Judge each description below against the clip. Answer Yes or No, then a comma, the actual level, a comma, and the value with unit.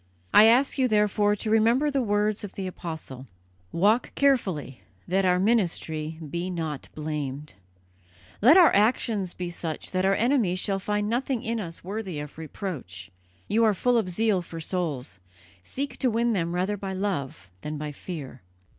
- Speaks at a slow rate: No, average, 165 wpm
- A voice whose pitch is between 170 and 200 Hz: Yes, high, 190 Hz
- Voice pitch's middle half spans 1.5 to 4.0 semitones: No, wide, 5.6 semitones